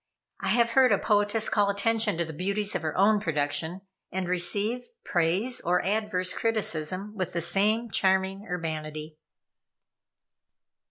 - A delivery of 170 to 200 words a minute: No, average, 140 wpm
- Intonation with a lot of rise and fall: No, average, 3.8 semitones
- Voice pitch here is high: Yes, high, 195 Hz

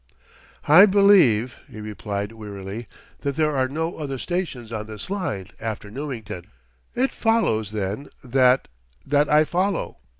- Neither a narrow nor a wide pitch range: No, wide, 6.7 semitones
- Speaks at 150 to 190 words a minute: No, slow, 135 wpm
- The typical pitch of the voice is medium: No, low, 130 Hz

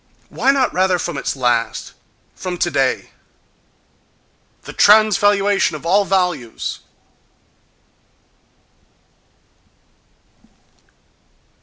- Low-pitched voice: No, medium, 180 Hz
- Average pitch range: No, wide, 6.4 semitones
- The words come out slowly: Yes, slow, 55 wpm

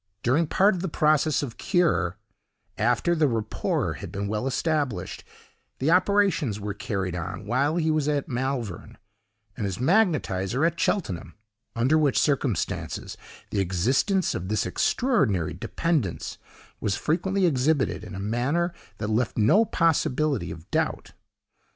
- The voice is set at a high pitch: No, low, 130 Hz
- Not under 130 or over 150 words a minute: Yes, average, 140 wpm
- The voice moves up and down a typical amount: No, wide, 7.8 semitones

